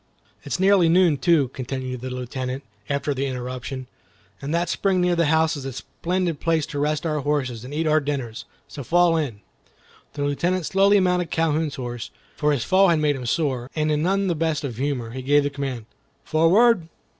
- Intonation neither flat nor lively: Yes, average, 4.2 semitones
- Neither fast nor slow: Yes, average, 195 wpm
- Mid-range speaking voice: Yes, medium, 150 Hz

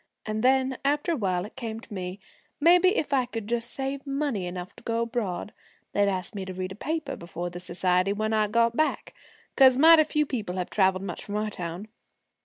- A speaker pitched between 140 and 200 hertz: No, high, 220 Hz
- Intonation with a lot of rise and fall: Yes, wide, 6.3 semitones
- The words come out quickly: Yes, fast, 210 wpm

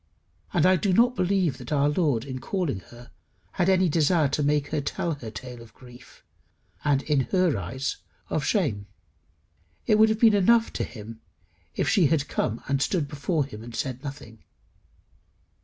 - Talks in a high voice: No, medium, 145 Hz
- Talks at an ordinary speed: Yes, average, 175 wpm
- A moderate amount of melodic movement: No, wide, 6.5 semitones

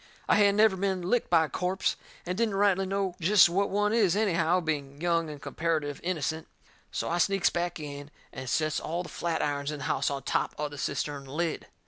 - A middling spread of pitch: Yes, average, 4.4 semitones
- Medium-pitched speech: Yes, medium, 170 Hz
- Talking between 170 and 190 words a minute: No, fast, 205 wpm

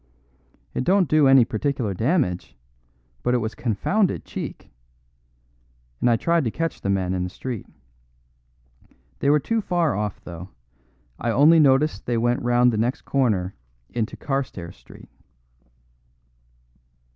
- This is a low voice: Yes, low, 125 Hz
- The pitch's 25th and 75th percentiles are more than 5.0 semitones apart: Yes, wide, 5.6 semitones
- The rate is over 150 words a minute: No, slow, 135 wpm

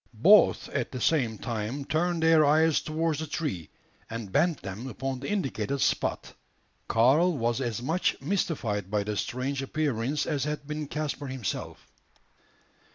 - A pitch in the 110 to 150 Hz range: Yes, medium, 140 Hz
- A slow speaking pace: No, average, 150 wpm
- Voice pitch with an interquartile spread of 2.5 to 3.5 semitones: No, average, 5.0 semitones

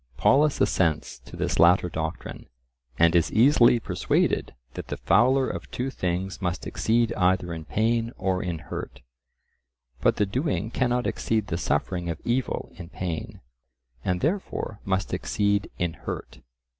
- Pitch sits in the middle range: No, very low, 95 Hz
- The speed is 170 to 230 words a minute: No, average, 145 wpm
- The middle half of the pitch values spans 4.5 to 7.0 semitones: Yes, average, 5.2 semitones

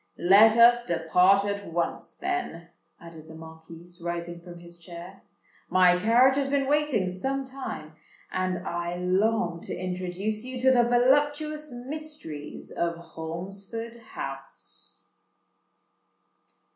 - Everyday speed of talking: No, slow, 120 wpm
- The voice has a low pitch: No, medium, 185 Hz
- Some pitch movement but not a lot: No, wide, 6.1 semitones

